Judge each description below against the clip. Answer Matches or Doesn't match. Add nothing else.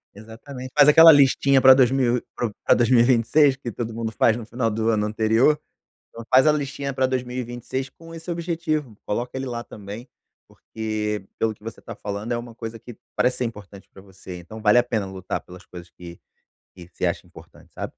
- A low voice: Matches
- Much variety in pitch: Doesn't match